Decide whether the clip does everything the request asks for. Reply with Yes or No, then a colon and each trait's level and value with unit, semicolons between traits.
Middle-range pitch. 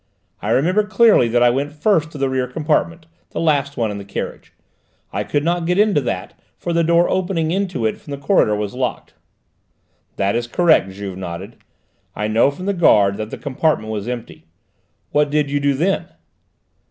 Yes: medium, 145 Hz